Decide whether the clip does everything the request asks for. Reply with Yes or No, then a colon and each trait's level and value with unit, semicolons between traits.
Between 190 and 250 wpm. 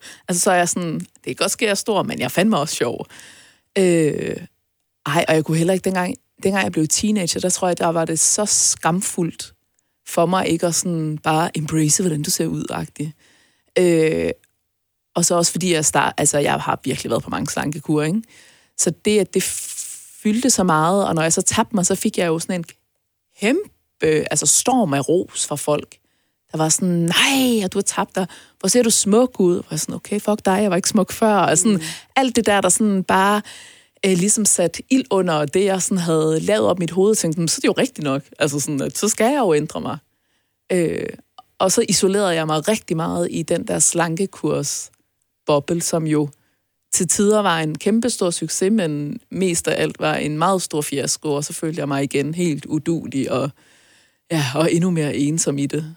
Yes: average, 215 wpm